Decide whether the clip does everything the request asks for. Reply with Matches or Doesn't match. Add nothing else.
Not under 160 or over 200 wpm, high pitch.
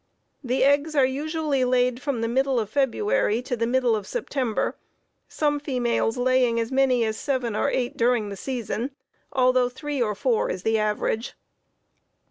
Matches